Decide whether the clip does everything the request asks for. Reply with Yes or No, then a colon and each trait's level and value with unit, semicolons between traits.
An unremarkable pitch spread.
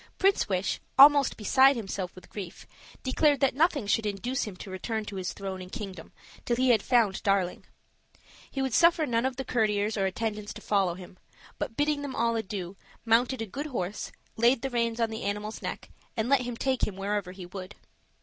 Yes: average, 4.7 semitones